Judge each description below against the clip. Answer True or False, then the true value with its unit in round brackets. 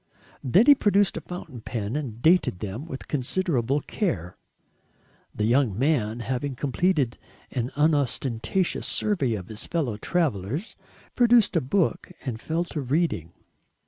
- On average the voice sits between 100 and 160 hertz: True (140 Hz)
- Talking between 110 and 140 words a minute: True (135 wpm)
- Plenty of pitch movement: True (6.8 semitones)